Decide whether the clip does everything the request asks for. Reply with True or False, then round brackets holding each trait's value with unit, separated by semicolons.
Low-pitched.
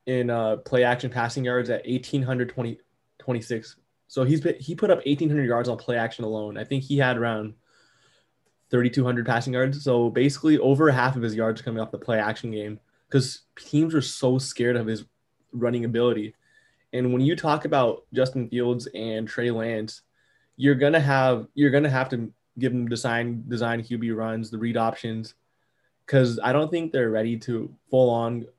True (120 Hz)